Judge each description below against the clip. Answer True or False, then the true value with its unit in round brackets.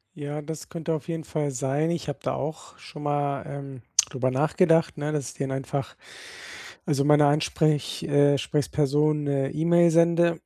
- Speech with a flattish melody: True (2.0 semitones)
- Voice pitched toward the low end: False (150 Hz)